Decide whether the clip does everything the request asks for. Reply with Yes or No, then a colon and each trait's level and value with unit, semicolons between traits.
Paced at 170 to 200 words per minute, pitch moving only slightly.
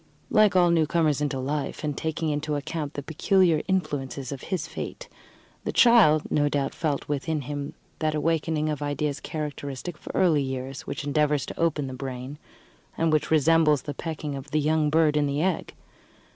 Yes: average, 175 wpm; narrow, 2.0 semitones